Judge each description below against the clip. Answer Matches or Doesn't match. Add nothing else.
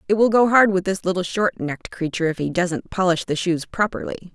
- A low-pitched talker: Doesn't match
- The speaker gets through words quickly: Matches